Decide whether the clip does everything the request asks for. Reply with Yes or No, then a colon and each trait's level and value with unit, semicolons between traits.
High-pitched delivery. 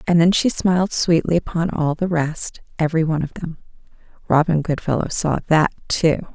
No: medium, 165 Hz